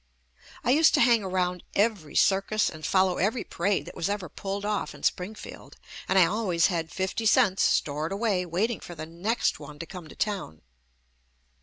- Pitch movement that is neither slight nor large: Yes, average, 3.8 semitones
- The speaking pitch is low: No, high, 190 Hz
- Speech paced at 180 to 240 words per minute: Yes, average, 185 wpm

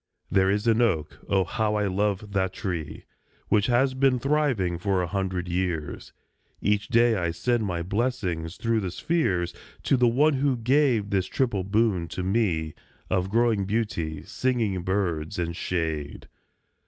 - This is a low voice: Yes, low, 100 Hz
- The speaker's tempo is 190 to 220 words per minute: No, average, 155 wpm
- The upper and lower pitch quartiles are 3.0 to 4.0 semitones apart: No, average, 4.7 semitones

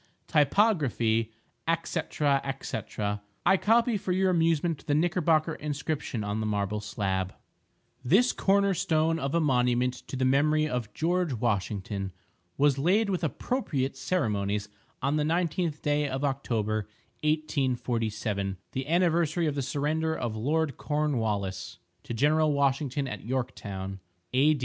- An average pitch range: No, wide, 5.7 semitones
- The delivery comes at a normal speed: No, slow, 130 wpm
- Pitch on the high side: No, medium, 140 Hz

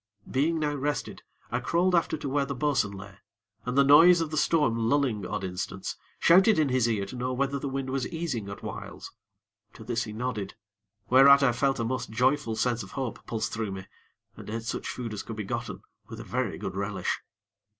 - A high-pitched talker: No, low, 125 Hz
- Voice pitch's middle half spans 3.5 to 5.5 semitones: Yes, average, 4.4 semitones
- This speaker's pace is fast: Yes, fast, 210 wpm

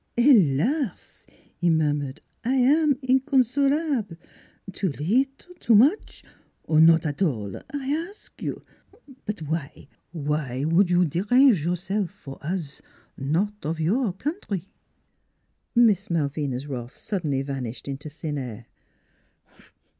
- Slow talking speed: Yes, slow, 125 wpm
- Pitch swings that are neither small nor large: No, wide, 9.0 semitones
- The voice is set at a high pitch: No, medium, 175 Hz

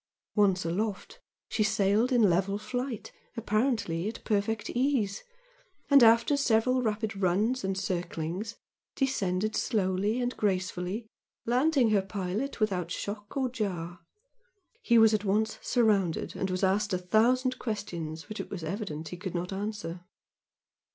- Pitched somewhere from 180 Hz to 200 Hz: No, high, 210 Hz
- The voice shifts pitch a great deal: No, average, 3.7 semitones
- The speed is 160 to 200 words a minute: No, average, 140 wpm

